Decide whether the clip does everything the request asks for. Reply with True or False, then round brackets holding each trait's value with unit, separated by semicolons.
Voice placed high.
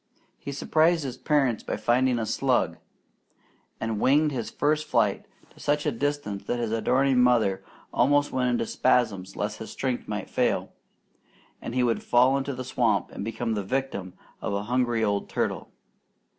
False (125 Hz)